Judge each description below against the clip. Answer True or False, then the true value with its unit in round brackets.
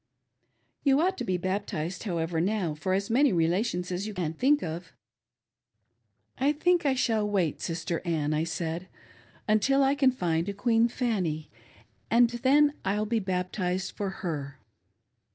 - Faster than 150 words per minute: True (165 wpm)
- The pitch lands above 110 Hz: True (190 Hz)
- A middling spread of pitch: False (5.9 semitones)